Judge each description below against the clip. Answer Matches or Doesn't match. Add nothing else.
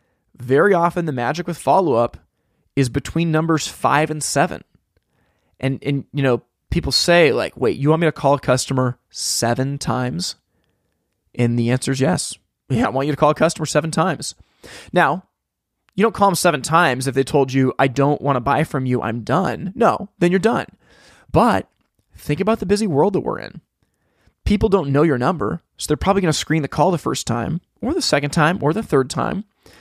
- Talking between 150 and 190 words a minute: Doesn't match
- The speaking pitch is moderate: Matches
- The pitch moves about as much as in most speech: Matches